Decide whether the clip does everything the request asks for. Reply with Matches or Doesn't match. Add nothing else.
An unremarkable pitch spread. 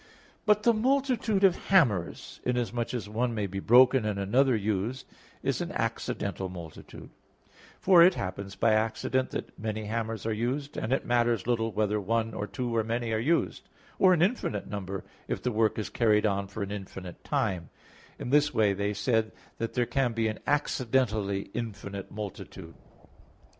Matches